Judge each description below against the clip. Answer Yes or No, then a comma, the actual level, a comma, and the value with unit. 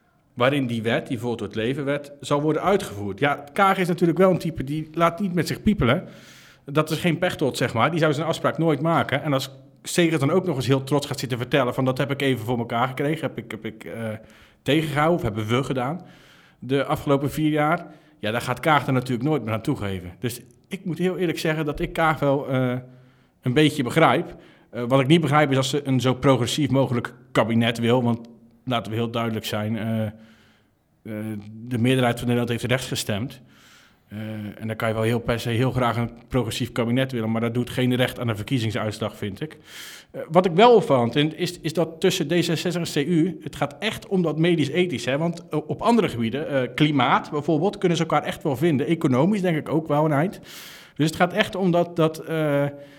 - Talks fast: Yes, fast, 225 wpm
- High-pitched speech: No, medium, 140 Hz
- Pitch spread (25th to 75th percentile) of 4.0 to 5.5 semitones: Yes, average, 5.0 semitones